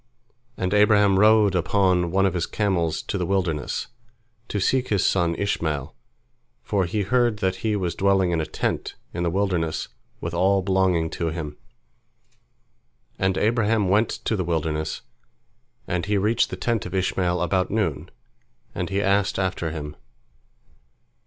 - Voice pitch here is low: Yes, very low, 95 Hz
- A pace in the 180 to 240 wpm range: No, average, 150 wpm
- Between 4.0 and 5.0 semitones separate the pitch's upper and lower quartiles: No, average, 3.1 semitones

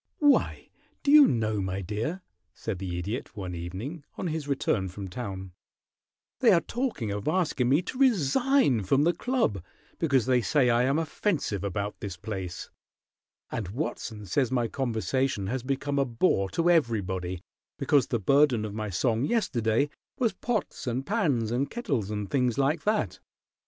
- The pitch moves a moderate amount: No, wide, 6.9 semitones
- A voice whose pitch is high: No, low, 125 Hz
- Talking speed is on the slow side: No, average, 160 wpm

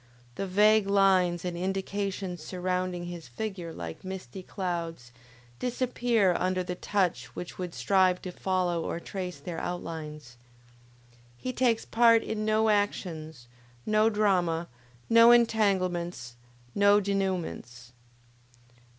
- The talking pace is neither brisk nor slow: No, slow, 115 wpm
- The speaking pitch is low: No, medium, 185 Hz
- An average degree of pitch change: Yes, average, 3.0 semitones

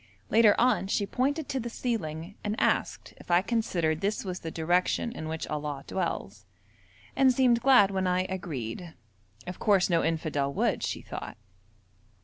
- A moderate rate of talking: Yes, average, 160 wpm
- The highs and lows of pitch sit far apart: Yes, wide, 6.1 semitones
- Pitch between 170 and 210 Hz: Yes, medium, 185 Hz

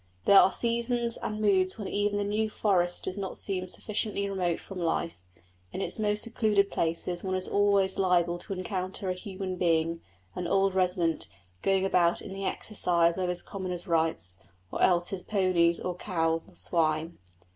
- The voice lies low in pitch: No, medium, 185 Hz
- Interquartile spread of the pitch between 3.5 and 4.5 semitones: No, narrow, 2.6 semitones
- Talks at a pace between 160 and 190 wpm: Yes, average, 175 wpm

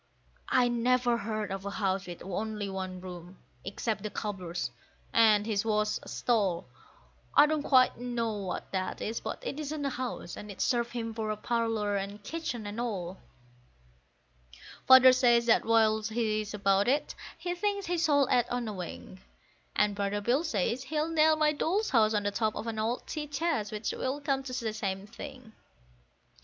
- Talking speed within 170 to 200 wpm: Yes, average, 180 wpm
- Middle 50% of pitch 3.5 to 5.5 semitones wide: Yes, average, 4.0 semitones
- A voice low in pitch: No, high, 225 Hz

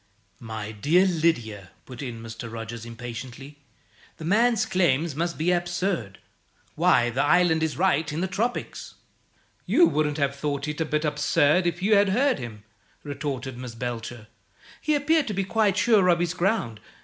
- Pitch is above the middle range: No, medium, 150 Hz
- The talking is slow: No, average, 165 wpm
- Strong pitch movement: Yes, wide, 7.1 semitones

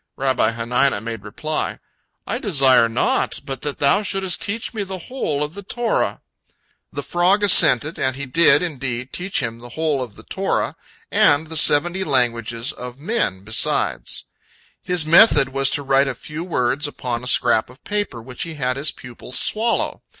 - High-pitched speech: No, medium, 140 Hz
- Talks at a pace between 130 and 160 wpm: No, average, 170 wpm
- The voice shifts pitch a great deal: Yes, wide, 5.8 semitones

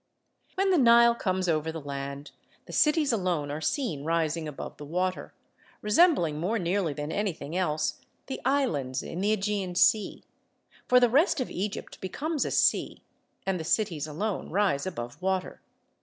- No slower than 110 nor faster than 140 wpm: No, average, 160 wpm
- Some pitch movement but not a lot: No, wide, 6.4 semitones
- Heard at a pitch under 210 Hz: Yes, medium, 185 Hz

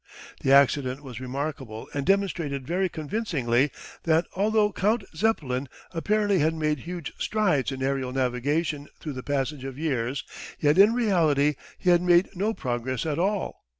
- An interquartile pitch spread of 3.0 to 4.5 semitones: No, average, 5.3 semitones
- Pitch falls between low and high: Yes, medium, 150 Hz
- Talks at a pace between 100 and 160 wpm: Yes, average, 150 wpm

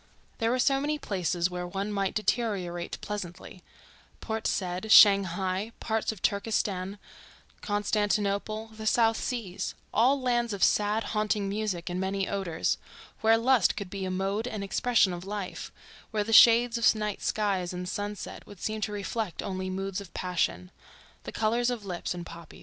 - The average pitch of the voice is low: No, high, 205 Hz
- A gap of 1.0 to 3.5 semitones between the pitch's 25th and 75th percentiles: Yes, average, 3.0 semitones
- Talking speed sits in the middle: Yes, average, 160 wpm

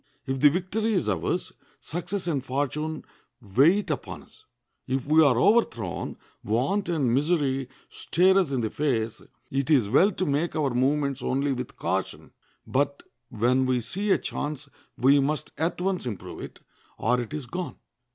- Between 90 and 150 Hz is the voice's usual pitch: Yes, medium, 140 Hz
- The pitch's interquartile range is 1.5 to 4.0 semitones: No, average, 4.9 semitones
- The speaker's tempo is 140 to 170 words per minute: Yes, average, 160 wpm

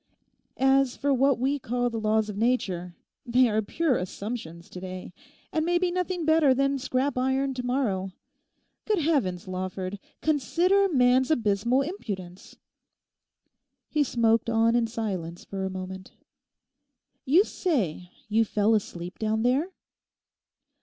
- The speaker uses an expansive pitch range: Yes, wide, 5.9 semitones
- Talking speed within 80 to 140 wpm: Yes, slow, 135 wpm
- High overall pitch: Yes, high, 240 Hz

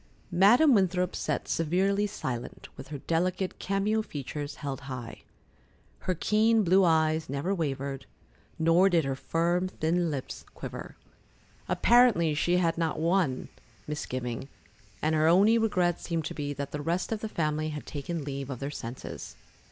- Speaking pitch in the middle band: Yes, medium, 165 Hz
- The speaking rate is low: No, average, 150 wpm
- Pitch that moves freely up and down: No, average, 4.5 semitones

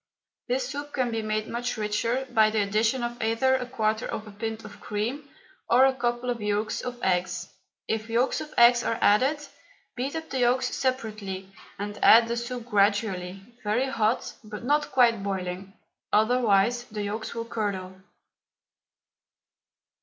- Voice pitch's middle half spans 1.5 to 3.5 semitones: Yes, average, 2.9 semitones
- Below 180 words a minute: Yes, average, 160 wpm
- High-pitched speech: Yes, high, 225 Hz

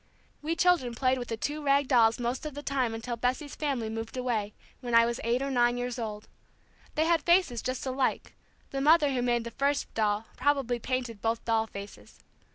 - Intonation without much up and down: No, average, 3.3 semitones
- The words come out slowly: No, average, 200 wpm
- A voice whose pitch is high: Yes, very high, 250 Hz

